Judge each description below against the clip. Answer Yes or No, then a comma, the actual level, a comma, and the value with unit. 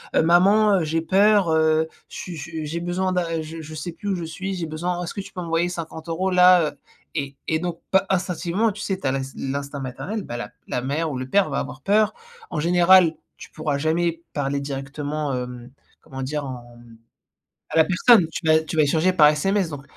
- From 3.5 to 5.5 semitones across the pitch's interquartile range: Yes, average, 3.8 semitones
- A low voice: No, medium, 160 Hz